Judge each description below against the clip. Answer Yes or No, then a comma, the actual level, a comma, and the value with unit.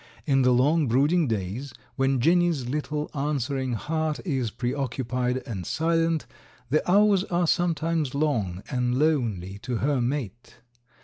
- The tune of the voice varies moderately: Yes, average, 4.3 semitones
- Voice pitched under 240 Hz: Yes, low, 135 Hz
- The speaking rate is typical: No, slow, 130 wpm